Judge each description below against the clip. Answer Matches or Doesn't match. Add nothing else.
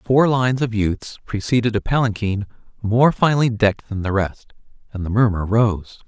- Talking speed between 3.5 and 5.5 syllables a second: Matches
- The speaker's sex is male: Matches